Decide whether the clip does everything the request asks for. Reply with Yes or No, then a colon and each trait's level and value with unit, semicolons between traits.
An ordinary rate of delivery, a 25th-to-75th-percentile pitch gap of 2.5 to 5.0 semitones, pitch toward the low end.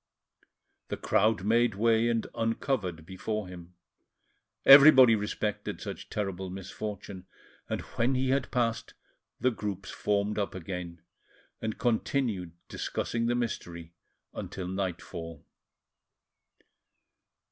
No: slow, 105 wpm; average, 4.0 semitones; low, 105 Hz